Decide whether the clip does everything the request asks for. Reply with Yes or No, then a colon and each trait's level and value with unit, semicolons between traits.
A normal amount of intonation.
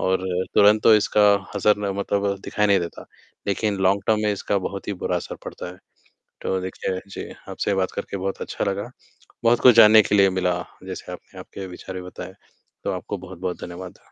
No: narrow, 1.9 semitones